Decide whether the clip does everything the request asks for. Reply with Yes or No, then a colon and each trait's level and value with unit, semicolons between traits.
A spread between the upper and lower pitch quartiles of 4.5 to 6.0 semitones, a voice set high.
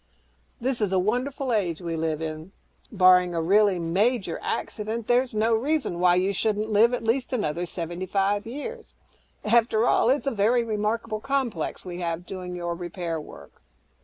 Yes: average, 4.9 semitones; high, 205 Hz